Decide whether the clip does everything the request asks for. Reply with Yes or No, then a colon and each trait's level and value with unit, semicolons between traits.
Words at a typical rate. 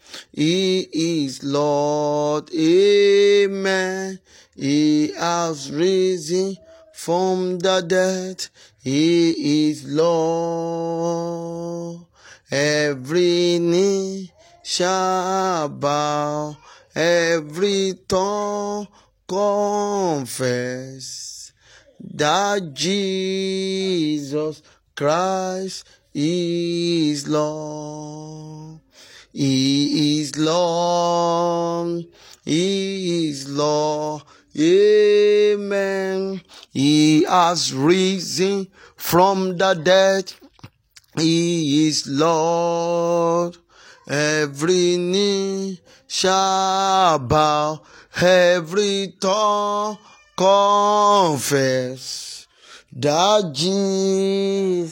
No: slow, 55 wpm